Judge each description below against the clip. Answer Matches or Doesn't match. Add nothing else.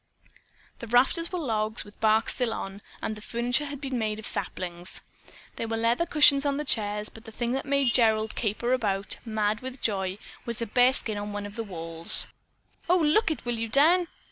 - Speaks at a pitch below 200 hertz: Doesn't match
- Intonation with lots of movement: Doesn't match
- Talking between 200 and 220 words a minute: Matches